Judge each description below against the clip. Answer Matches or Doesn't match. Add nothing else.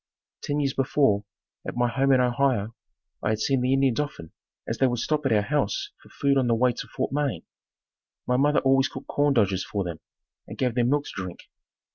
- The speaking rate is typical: Doesn't match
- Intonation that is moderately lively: Matches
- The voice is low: Matches